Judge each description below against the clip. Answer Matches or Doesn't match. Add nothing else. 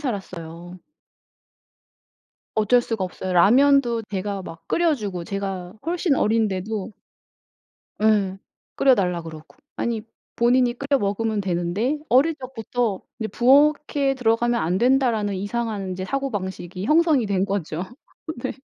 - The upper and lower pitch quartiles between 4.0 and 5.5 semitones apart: Matches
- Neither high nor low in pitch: Doesn't match